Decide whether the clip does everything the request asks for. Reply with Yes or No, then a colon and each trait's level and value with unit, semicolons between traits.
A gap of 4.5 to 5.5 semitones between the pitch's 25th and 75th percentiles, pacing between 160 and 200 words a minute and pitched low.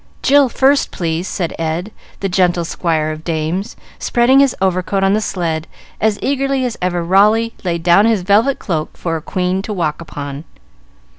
No: average, 4.8 semitones; average, 175 wpm; medium, 185 Hz